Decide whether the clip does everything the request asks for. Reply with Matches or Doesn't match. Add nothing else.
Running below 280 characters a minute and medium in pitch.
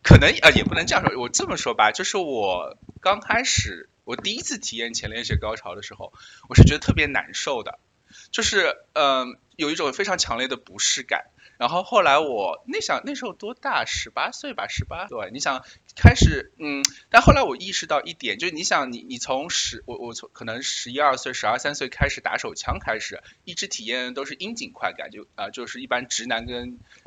Doesn't match